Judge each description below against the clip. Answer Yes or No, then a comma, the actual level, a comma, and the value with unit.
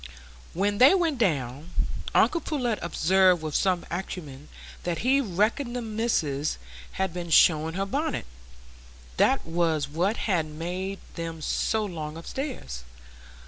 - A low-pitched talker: No, medium, 175 Hz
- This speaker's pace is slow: Yes, slow, 125 wpm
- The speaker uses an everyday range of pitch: No, wide, 5.9 semitones